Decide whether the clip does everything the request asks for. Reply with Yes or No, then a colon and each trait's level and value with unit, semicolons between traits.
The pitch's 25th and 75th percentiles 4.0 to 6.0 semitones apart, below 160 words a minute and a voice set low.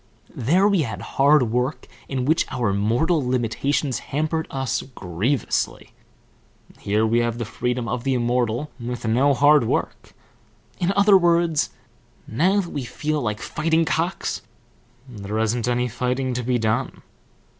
Yes: average, 4.4 semitones; average, 145 wpm; low, 125 Hz